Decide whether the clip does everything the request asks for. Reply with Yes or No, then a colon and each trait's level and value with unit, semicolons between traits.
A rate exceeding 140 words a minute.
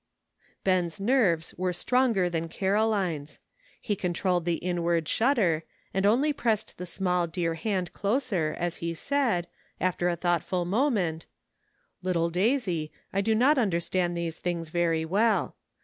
No: slow, 135 wpm